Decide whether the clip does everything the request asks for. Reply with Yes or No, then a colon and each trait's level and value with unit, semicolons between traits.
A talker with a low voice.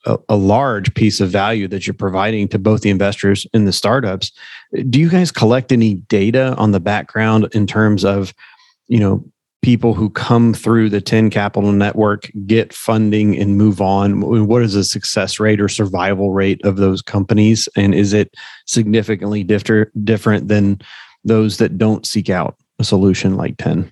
Yes: low, 105 Hz